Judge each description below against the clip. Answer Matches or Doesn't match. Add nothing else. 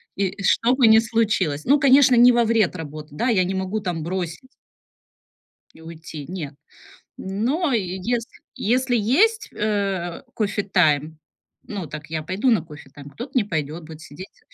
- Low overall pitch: Doesn't match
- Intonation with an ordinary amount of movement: Doesn't match